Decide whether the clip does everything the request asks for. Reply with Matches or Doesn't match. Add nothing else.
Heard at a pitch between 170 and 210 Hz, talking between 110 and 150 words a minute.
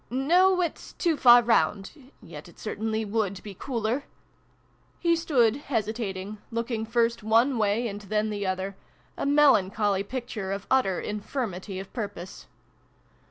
Doesn't match